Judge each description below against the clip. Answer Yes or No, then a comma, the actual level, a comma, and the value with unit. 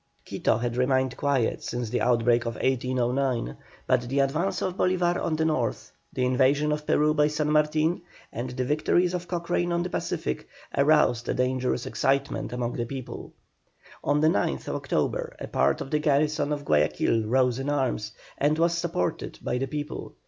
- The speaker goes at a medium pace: Yes, average, 175 wpm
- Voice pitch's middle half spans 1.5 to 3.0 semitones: No, average, 3.7 semitones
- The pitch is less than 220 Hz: Yes, medium, 140 Hz